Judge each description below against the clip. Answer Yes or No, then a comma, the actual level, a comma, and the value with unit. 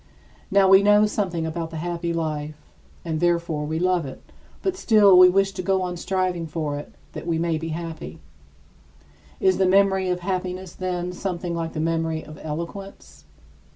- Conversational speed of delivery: Yes, average, 175 wpm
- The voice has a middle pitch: Yes, medium, 175 Hz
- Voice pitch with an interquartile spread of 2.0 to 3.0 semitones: Yes, average, 2.7 semitones